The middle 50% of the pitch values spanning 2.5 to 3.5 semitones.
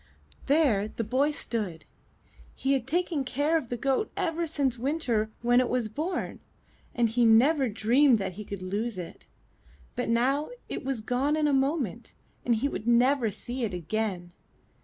No: average, 4.4 semitones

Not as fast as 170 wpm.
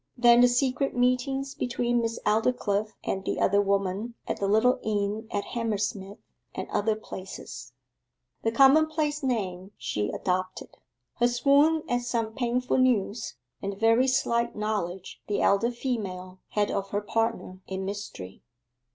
Yes: average, 145 wpm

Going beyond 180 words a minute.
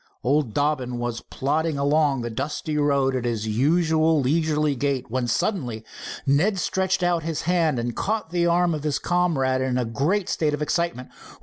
No: average, 175 wpm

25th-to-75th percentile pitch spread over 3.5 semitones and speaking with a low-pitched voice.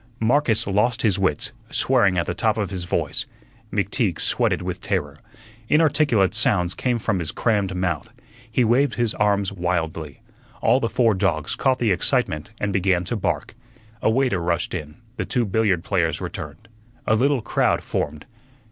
Yes: average, 4.7 semitones; low, 100 Hz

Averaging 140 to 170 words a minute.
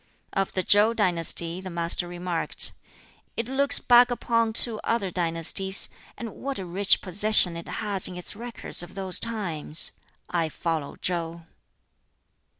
Yes: average, 145 wpm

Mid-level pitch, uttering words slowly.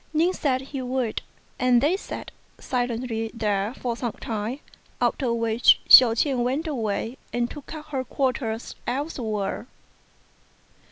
No: high, 245 Hz; slow, 130 wpm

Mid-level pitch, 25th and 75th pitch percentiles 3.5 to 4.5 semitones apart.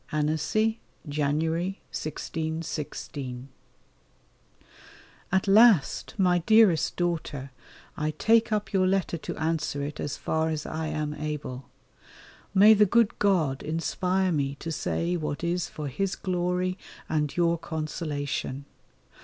Yes: medium, 160 Hz; average, 3.8 semitones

